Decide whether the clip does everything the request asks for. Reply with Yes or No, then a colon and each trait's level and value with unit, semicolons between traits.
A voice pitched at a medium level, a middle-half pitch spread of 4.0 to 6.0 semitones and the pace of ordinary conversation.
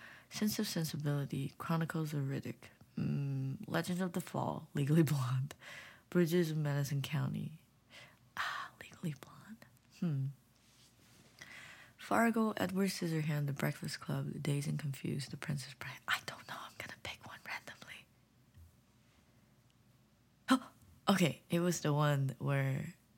No: medium, 145 Hz; average, 5.2 semitones; slow, 125 wpm